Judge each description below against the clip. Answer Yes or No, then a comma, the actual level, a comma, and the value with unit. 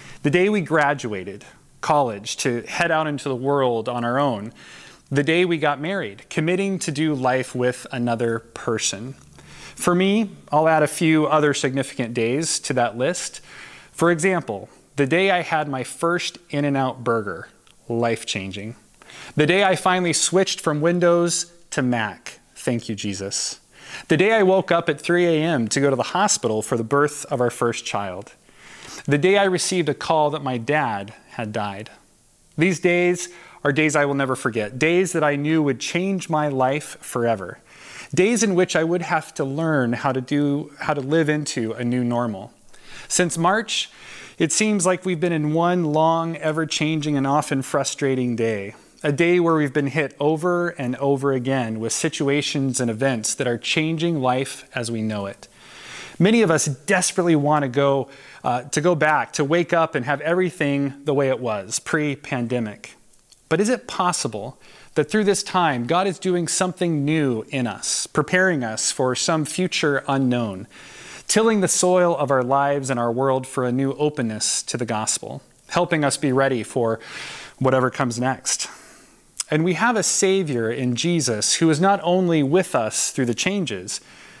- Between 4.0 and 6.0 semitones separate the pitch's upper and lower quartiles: Yes, average, 5.3 semitones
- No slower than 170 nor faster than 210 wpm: Yes, average, 180 wpm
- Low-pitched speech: No, medium, 145 Hz